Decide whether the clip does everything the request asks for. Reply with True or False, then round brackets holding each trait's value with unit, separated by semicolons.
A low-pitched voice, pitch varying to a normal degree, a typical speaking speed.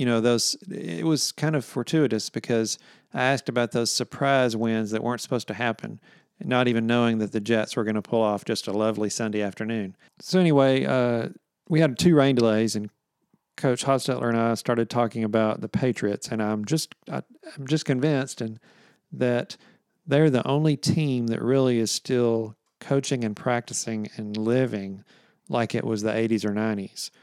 True (120 Hz; 3.5 semitones; 185 wpm)